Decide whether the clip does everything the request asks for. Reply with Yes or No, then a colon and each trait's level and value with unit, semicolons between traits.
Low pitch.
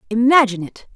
No: high, 230 Hz